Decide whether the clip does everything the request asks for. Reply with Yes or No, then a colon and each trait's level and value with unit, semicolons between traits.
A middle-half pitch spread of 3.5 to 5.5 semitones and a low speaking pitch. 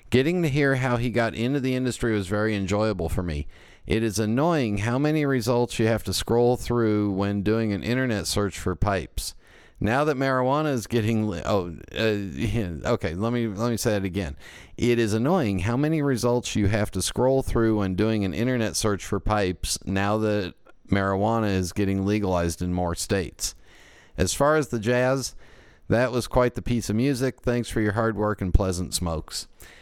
Yes: average, 3.8 semitones; low, 110 Hz